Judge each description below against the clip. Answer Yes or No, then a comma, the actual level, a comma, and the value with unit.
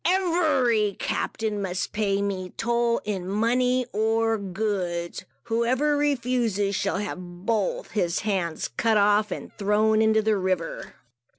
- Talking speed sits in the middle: No, slow, 125 wpm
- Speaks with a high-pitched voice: Yes, high, 215 Hz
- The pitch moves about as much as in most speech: Yes, average, 3.1 semitones